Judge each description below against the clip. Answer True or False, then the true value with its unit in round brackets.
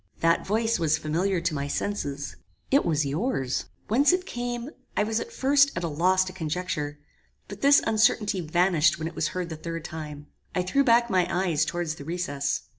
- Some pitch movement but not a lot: False (5.9 semitones)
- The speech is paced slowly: False (190 wpm)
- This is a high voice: False (175 Hz)